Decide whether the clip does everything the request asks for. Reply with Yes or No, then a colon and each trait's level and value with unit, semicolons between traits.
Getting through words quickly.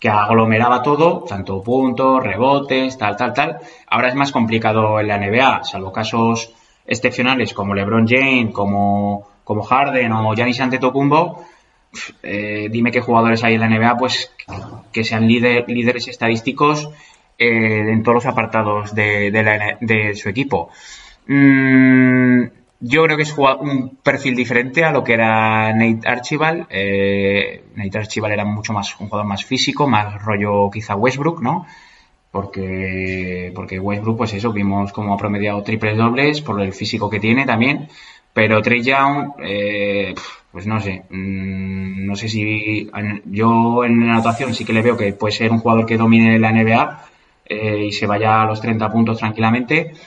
No: average, 165 wpm